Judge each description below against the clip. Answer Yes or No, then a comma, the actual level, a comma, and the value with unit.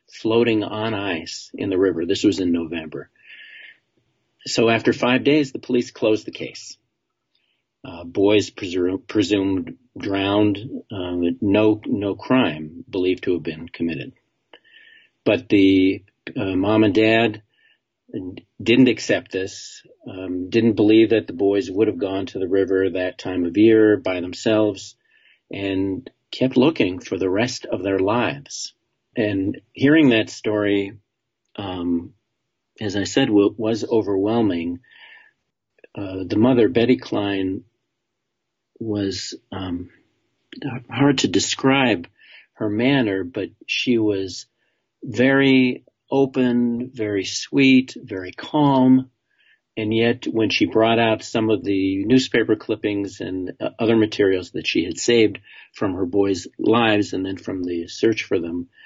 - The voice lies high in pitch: No, low, 105 Hz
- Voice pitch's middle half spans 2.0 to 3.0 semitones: No, average, 3.4 semitones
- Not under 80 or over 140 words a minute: Yes, slow, 135 wpm